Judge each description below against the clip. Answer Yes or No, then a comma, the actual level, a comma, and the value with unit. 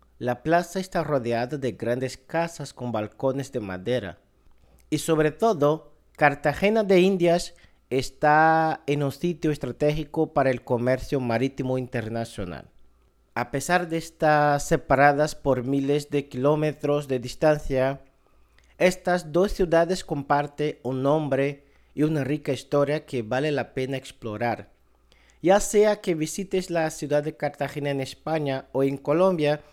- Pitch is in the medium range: Yes, medium, 145 Hz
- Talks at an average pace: Yes, average, 135 wpm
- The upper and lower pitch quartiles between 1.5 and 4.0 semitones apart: Yes, average, 3.6 semitones